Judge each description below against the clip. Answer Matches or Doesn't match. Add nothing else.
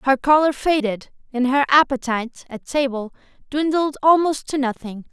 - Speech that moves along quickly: Doesn't match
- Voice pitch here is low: Doesn't match